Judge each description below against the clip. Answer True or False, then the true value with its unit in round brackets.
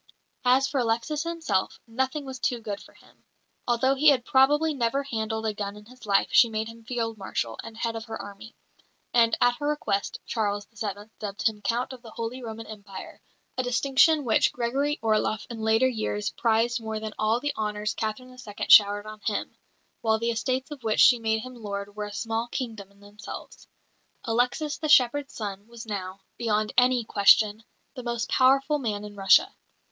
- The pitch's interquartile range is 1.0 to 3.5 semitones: True (3.1 semitones)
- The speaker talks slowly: False (190 wpm)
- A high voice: True (225 Hz)